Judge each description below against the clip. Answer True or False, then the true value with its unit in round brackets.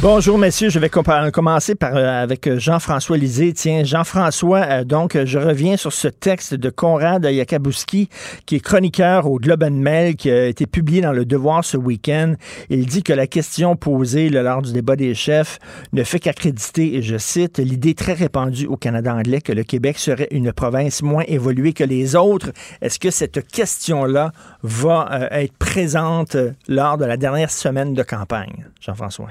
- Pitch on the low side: False (150 Hz)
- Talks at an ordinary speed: True (180 wpm)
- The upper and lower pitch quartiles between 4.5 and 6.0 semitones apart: False (4.0 semitones)